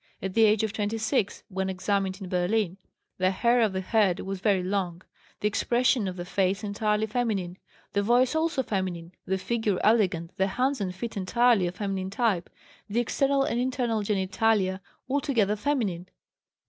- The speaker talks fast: No, average, 165 wpm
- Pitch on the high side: Yes, high, 205 Hz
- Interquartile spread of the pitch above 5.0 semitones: No, average, 3.6 semitones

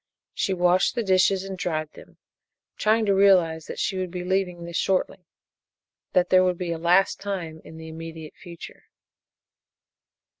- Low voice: No, medium, 180 Hz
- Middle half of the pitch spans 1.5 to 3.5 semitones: Yes, narrow, 2.5 semitones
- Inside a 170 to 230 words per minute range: No, average, 160 wpm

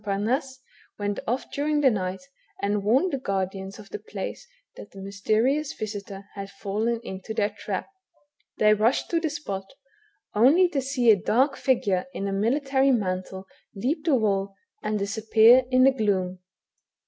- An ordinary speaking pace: Yes, average, 160 wpm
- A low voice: No, high, 215 Hz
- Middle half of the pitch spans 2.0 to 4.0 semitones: No, average, 5.0 semitones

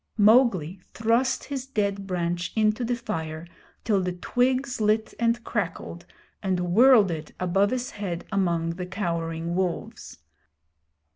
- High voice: Yes, high, 195 Hz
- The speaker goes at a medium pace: No, slow, 130 wpm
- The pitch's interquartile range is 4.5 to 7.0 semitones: Yes, average, 5.0 semitones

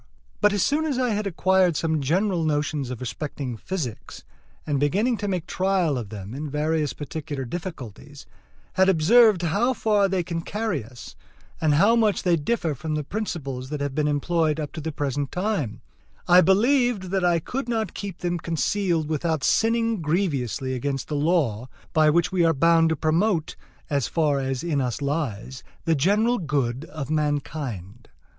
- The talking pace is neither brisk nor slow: Yes, average, 170 wpm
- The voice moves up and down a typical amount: Yes, average, 4.9 semitones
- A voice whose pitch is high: No, medium, 160 Hz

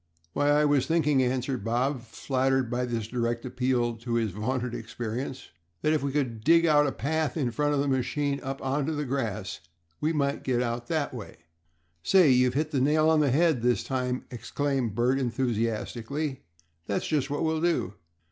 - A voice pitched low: Yes, low, 130 Hz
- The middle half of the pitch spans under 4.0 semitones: Yes, average, 3.6 semitones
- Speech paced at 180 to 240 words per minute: Yes, average, 185 wpm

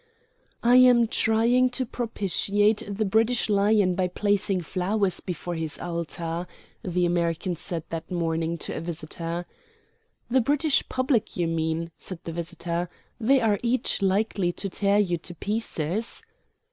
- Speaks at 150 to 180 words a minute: No, average, 140 wpm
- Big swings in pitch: No, average, 4.6 semitones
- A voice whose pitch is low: No, high, 190 Hz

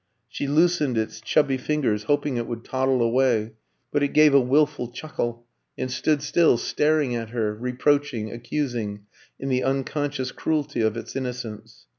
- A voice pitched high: No, low, 130 Hz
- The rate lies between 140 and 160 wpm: Yes, average, 155 wpm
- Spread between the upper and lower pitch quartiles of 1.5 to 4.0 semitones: Yes, average, 3.7 semitones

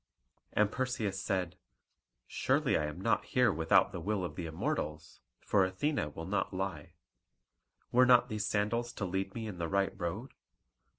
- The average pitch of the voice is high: No, very low, 95 Hz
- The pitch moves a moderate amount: Yes, average, 4.0 semitones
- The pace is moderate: Yes, average, 165 wpm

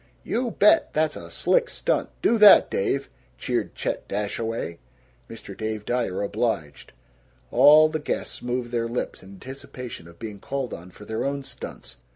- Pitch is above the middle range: No, low, 120 Hz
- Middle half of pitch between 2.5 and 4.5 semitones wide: No, average, 5.3 semitones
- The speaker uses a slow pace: No, average, 160 wpm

